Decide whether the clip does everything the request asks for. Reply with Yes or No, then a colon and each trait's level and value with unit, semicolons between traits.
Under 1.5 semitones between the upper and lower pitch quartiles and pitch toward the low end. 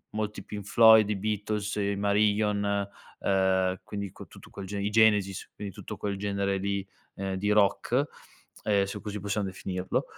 Yes: narrow, 1.1 semitones; low, 100 Hz